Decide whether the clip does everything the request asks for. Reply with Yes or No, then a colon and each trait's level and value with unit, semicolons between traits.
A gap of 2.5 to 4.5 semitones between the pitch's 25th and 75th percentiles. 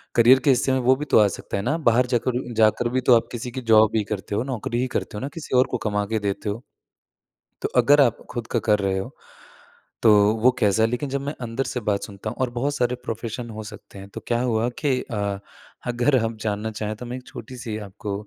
Yes: average, 3.0 semitones